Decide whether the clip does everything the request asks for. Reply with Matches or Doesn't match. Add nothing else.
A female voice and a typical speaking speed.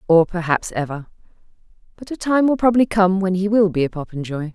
Matches